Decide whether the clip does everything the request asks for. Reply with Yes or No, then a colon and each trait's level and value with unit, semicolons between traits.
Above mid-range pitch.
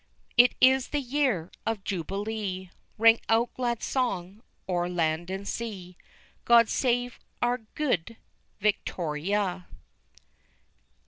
Yes: high, 210 Hz